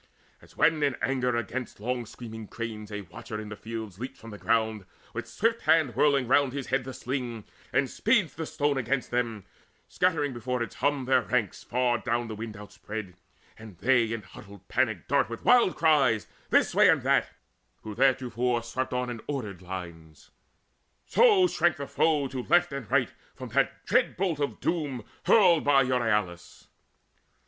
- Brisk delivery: No, average, 175 wpm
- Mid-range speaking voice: No, low, 125 Hz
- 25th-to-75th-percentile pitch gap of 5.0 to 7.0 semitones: No, average, 4.3 semitones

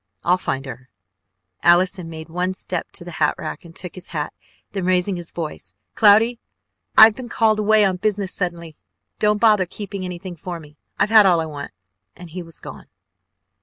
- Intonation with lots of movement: No, average, 3.8 semitones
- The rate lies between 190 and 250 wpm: Yes, average, 195 wpm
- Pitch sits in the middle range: Yes, medium, 180 Hz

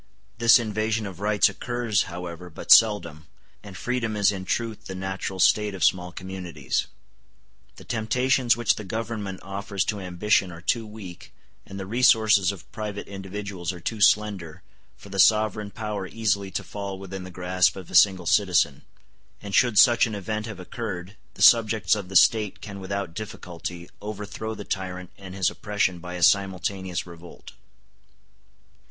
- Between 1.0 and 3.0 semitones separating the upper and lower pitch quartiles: Yes, average, 2.7 semitones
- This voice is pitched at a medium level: No, low, 100 Hz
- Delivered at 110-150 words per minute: No, average, 160 wpm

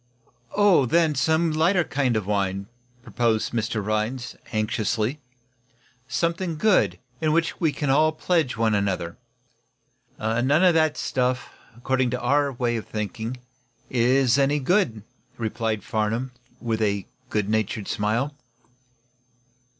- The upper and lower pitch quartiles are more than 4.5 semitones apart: Yes, wide, 5.5 semitones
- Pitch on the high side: No, low, 120 Hz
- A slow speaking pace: Yes, slow, 125 wpm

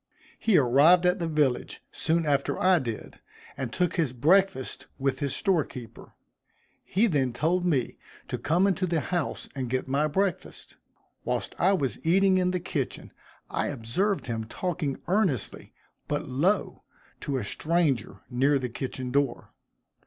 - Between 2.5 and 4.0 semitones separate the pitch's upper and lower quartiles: No, wide, 5.6 semitones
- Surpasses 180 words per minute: No, average, 155 wpm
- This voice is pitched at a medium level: Yes, medium, 150 Hz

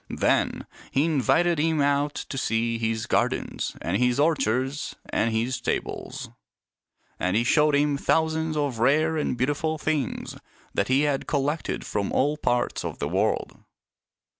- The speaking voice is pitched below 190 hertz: Yes, medium, 140 Hz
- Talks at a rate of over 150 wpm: No, average, 145 wpm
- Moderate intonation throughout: Yes, average, 4.0 semitones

